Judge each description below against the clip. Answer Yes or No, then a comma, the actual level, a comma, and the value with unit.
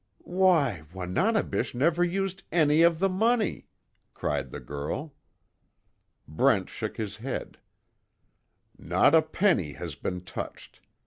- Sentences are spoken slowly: Yes, slow, 115 wpm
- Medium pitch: Yes, medium, 160 Hz